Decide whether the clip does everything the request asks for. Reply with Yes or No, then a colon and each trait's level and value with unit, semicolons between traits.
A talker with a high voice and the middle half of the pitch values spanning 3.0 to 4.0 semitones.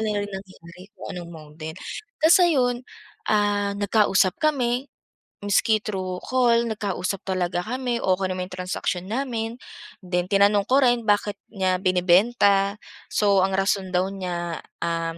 Yes: high, 200 Hz; average, 3.5 semitones